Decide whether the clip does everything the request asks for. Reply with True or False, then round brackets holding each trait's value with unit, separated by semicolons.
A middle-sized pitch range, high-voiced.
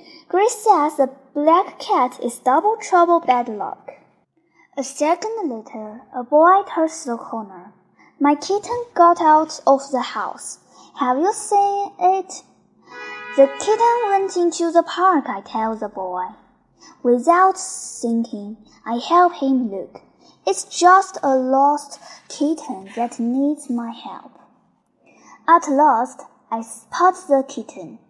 False (6.6 semitones; 295 Hz)